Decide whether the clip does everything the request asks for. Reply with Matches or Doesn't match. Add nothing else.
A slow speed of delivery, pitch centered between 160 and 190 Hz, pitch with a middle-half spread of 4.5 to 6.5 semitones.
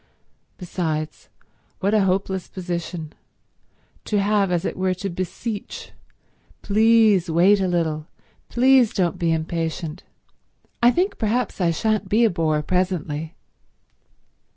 Doesn't match